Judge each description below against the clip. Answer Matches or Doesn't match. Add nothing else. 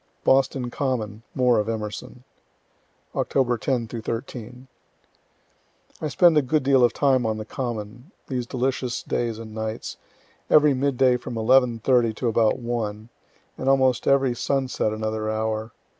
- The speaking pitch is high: Doesn't match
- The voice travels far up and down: Doesn't match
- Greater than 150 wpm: Doesn't match